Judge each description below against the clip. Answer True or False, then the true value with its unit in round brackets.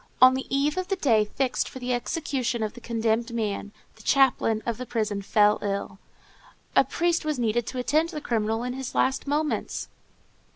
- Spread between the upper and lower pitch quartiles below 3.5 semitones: False (3.9 semitones)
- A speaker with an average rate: True (190 wpm)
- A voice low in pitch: False (245 Hz)